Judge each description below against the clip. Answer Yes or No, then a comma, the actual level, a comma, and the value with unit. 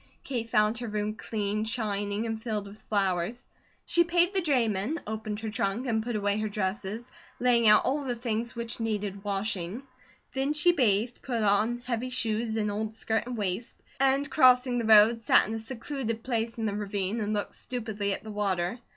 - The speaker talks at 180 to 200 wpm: Yes, average, 190 wpm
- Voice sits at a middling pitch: No, high, 220 Hz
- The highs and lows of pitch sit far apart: No, average, 2.7 semitones